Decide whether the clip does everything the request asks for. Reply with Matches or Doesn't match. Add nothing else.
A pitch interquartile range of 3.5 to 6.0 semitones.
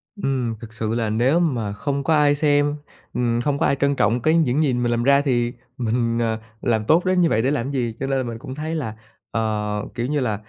Matches